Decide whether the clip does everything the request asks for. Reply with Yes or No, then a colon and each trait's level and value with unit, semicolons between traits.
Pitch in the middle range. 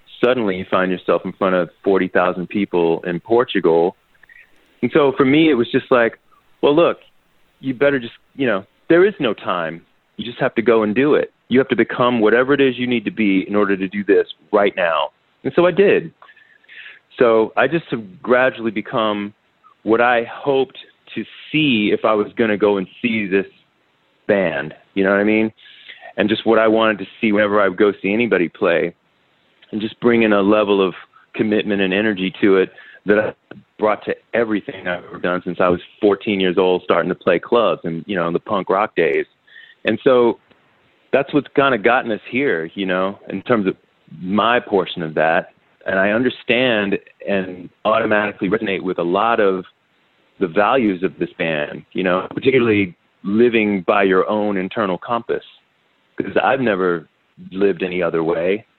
No: low, 105 Hz